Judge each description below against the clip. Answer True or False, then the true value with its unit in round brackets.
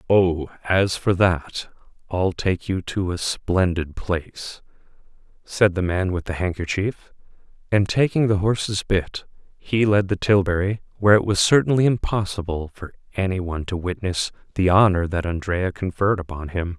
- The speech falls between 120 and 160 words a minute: True (155 wpm)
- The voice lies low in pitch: True (95 Hz)